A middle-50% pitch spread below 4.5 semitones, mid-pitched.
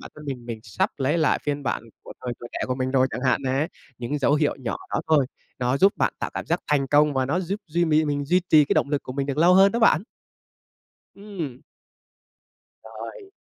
Yes: average, 3.9 semitones; medium, 145 Hz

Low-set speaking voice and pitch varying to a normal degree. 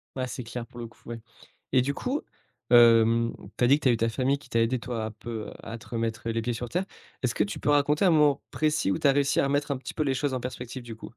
Yes: low, 125 Hz; average, 3.5 semitones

